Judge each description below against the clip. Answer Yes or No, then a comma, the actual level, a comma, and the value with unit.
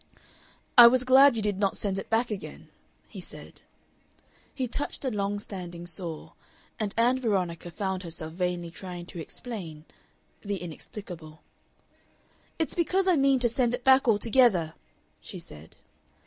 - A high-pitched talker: Yes, high, 205 Hz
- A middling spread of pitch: No, wide, 6.0 semitones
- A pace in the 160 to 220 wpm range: No, average, 150 wpm